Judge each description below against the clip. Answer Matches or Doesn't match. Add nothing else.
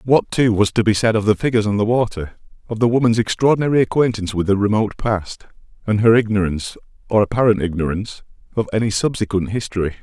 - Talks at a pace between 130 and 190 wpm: Matches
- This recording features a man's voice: Matches